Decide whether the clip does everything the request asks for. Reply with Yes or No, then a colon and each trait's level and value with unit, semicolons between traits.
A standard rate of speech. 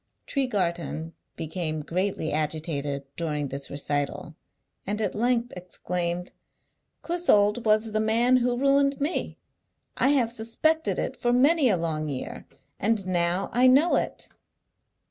No: slow, 125 wpm